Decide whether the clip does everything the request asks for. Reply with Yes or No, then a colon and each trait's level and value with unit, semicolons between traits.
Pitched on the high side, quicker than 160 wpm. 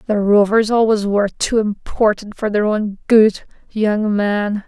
No: high, 210 Hz; average, 155 wpm